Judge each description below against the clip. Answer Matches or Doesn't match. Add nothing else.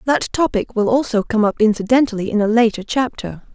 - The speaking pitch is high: Matches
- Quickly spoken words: Doesn't match